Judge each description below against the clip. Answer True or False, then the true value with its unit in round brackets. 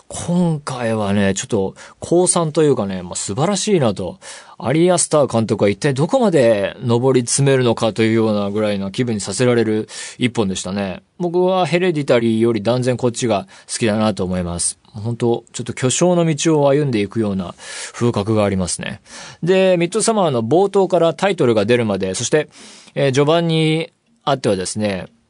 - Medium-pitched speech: False (120 Hz)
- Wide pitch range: True (7.3 semitones)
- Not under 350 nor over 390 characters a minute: True (370 characters per minute)